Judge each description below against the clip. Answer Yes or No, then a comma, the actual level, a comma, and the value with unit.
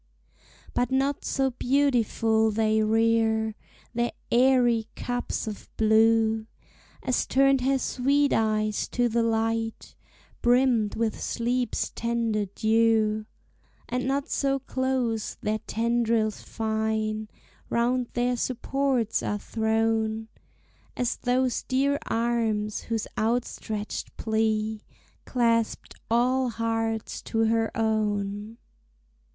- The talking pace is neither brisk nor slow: No, slow, 100 wpm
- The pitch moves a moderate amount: No, narrow, 2.1 semitones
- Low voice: No, high, 225 Hz